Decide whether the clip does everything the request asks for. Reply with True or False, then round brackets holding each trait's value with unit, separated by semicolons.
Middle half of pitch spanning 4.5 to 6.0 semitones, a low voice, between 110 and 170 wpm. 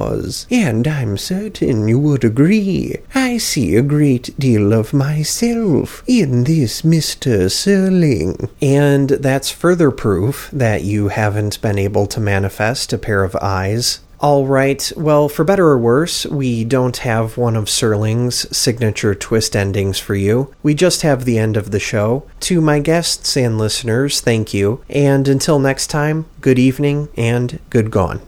True (5.3 semitones; 130 Hz; 155 wpm)